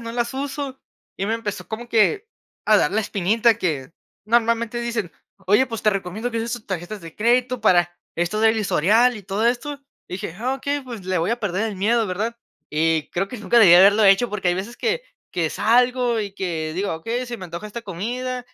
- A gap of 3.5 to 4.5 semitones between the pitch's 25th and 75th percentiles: Yes, average, 4.2 semitones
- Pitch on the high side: Yes, high, 220 Hz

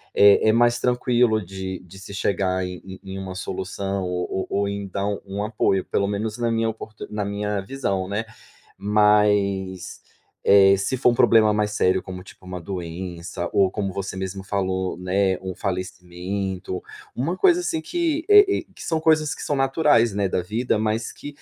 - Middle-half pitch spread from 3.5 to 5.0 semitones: No, average, 3.0 semitones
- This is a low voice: Yes, low, 100 Hz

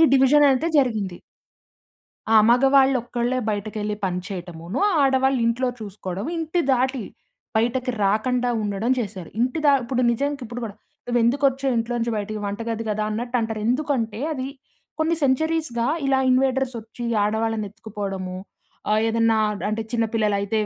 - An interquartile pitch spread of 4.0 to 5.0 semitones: No, average, 3.6 semitones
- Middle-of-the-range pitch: No, high, 235 Hz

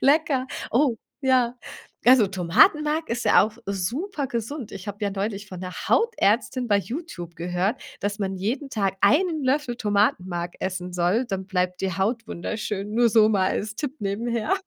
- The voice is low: No, high, 215 Hz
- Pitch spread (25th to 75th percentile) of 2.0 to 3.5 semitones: No, average, 5.1 semitones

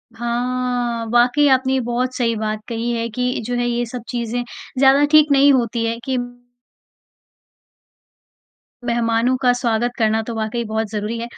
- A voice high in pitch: Yes, high, 240 Hz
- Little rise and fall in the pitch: Yes, narrow, 1.6 semitones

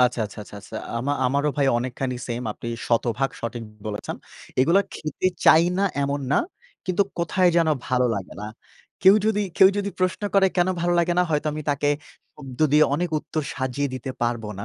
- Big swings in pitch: Yes, wide, 5.7 semitones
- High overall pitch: No, medium, 140 Hz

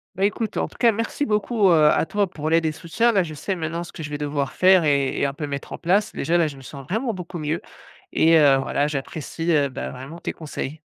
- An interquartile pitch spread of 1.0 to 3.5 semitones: No, average, 4.5 semitones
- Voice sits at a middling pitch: Yes, medium, 160 Hz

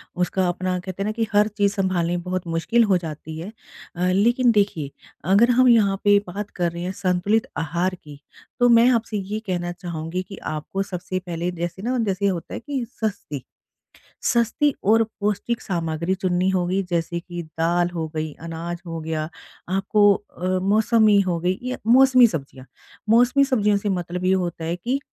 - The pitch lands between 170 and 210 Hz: Yes, medium, 185 Hz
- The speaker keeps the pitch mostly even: No, average, 3.5 semitones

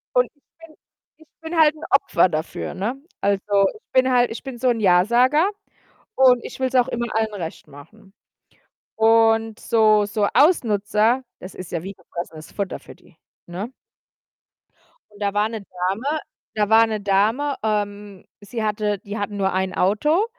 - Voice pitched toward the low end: No, high, 215 Hz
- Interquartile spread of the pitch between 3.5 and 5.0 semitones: Yes, average, 3.9 semitones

